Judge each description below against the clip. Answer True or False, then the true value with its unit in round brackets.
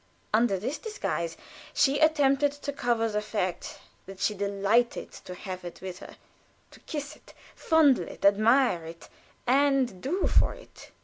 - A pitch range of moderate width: False (6.6 semitones)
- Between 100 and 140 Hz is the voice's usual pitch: False (235 Hz)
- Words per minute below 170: True (150 wpm)